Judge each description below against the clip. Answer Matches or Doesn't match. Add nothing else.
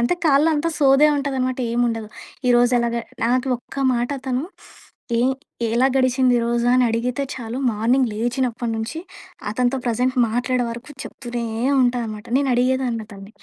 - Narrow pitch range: Matches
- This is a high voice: Matches